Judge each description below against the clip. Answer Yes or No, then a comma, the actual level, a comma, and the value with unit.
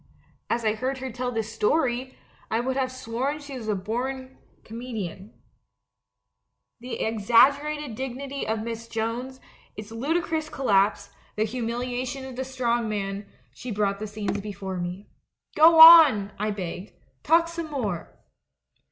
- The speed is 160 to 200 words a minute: No, average, 145 wpm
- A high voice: Yes, high, 235 Hz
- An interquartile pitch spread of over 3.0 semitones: Yes, average, 3.8 semitones